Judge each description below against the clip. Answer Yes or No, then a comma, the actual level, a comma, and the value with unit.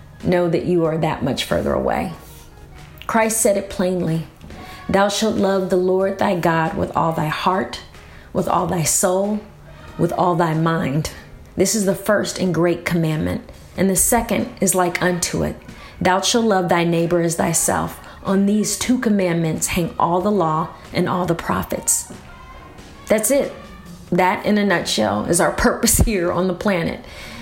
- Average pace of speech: Yes, average, 170 wpm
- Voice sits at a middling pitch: Yes, medium, 180 Hz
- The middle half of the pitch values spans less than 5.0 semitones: Yes, average, 3.4 semitones